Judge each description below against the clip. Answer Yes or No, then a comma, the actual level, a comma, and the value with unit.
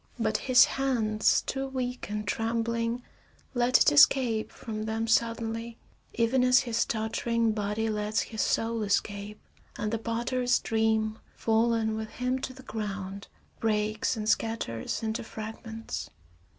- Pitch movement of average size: No, narrow, 1.5 semitones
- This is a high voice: Yes, high, 225 Hz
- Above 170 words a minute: No, slow, 135 wpm